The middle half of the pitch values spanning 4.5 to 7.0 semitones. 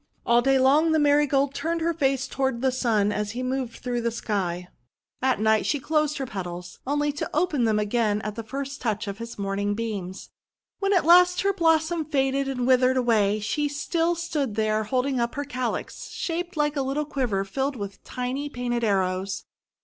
Yes: average, 5.2 semitones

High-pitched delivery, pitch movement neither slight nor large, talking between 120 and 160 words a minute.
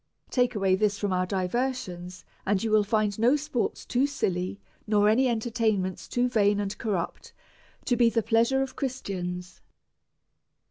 Yes: high, 215 Hz; average, 4.2 semitones; average, 150 wpm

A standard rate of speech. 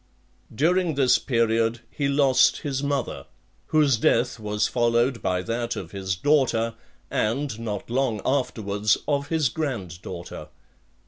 No: slow, 130 wpm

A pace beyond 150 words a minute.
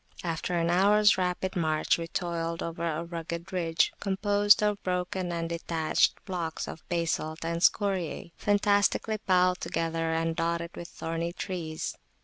No: average, 140 wpm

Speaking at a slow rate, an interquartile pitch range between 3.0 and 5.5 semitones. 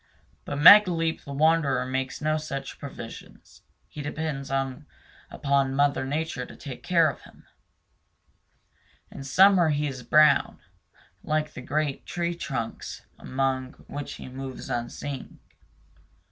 No: slow, 120 wpm; narrow, 2.6 semitones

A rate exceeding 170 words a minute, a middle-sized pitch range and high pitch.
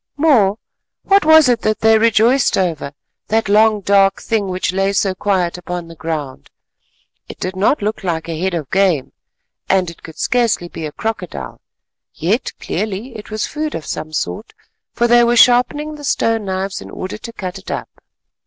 Yes: average, 180 wpm; average, 4.4 semitones; high, 200 Hz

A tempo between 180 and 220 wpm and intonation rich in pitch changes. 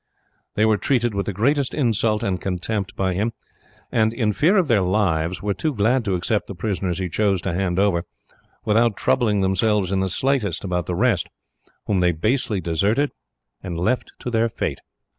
No: average, 185 wpm; average, 3.8 semitones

